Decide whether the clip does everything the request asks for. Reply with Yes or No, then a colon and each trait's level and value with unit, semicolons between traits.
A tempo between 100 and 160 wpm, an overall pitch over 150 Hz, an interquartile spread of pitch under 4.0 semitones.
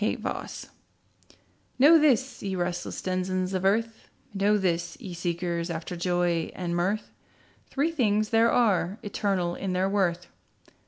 Yes: average, 140 wpm; high, 190 Hz; average, 3.4 semitones